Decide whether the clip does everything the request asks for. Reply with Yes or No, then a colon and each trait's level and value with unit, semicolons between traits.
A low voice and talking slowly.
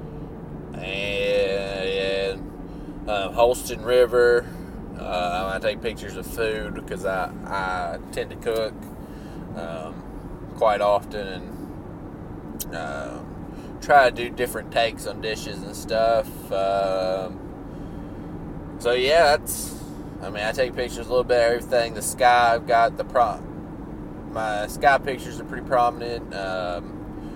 Yes: low, 105 Hz; slow, 125 wpm